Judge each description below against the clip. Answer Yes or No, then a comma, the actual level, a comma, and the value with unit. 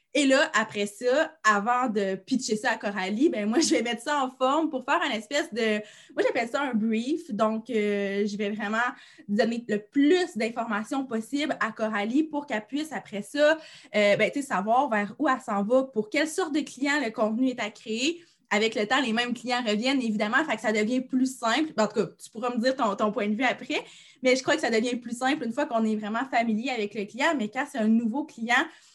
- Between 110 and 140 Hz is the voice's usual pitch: No, high, 240 Hz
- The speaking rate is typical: No, fast, 235 wpm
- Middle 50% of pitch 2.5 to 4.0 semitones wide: No, average, 4.6 semitones